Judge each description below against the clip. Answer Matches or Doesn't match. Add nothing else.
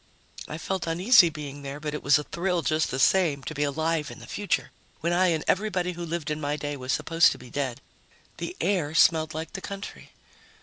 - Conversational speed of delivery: Doesn't match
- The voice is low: Doesn't match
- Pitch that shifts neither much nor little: Matches